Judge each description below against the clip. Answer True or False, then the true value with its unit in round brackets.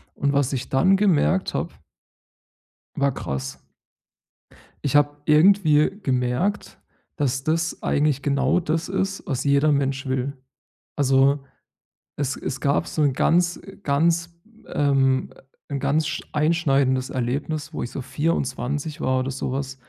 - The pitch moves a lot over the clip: False (2.9 semitones)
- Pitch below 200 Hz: True (140 Hz)